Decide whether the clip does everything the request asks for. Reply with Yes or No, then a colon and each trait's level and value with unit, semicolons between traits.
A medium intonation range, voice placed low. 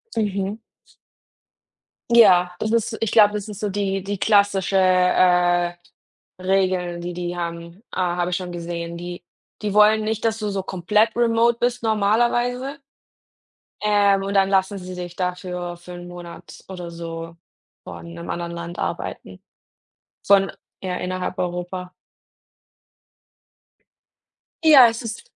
No: average, 3.2 semitones; high, 190 Hz